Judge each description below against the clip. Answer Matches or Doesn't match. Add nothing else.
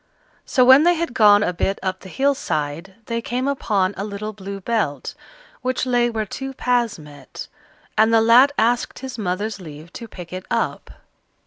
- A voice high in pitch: Matches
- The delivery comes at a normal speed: Matches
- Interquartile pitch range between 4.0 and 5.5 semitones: Matches